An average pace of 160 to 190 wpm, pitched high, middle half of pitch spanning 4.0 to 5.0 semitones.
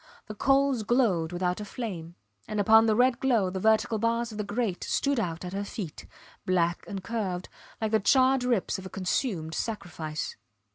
Yes: average, 185 wpm; high, 210 Hz; average, 4.4 semitones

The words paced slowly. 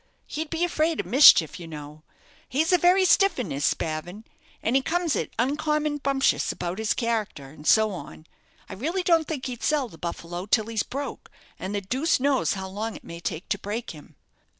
No: average, 200 wpm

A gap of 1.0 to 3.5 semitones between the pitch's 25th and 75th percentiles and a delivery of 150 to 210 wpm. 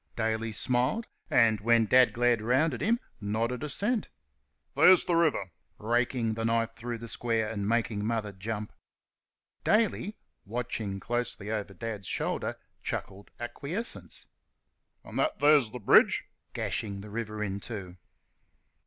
No: average, 2.8 semitones; slow, 135 wpm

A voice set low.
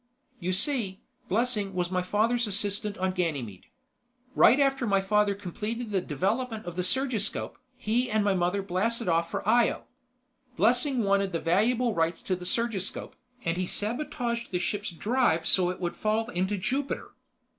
No: high, 205 Hz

